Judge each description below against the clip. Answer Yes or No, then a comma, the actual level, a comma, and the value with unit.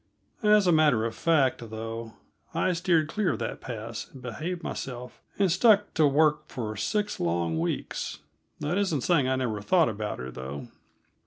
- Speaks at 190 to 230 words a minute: No, average, 170 wpm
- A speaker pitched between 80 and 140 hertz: Yes, low, 135 Hz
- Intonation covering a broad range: Yes, wide, 7.6 semitones